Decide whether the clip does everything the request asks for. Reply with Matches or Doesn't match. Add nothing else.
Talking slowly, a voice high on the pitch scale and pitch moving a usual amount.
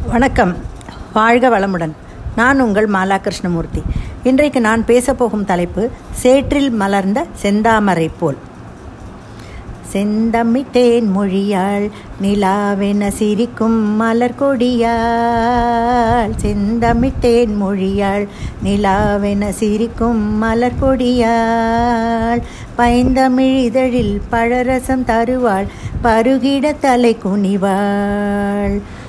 Matches